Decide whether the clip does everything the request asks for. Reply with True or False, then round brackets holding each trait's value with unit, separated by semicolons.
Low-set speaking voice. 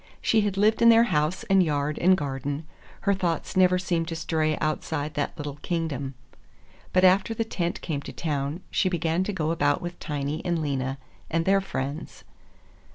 False (165 Hz)